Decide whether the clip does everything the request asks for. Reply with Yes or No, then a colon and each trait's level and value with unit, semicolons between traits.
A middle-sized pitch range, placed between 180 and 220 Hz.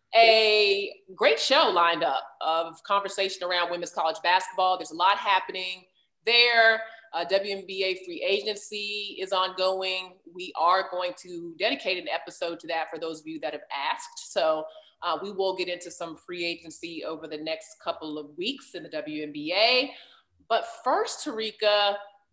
Yes: average, 3.9 semitones; medium, 185 Hz